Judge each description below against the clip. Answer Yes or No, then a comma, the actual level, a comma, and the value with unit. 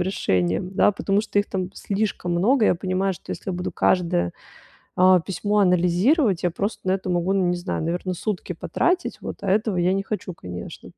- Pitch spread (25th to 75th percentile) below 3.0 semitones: Yes, narrow, 2.4 semitones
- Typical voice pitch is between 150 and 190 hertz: Yes, medium, 185 Hz